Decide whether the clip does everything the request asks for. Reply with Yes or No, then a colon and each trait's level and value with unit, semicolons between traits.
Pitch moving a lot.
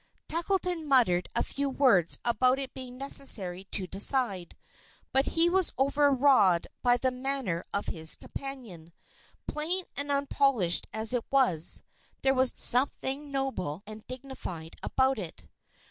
Yes: wide, 6.1 semitones